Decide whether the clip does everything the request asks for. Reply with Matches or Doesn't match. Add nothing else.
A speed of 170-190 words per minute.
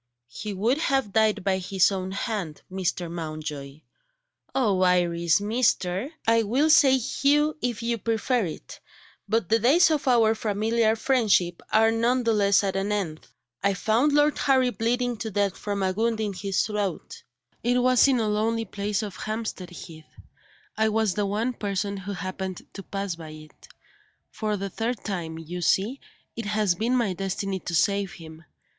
Matches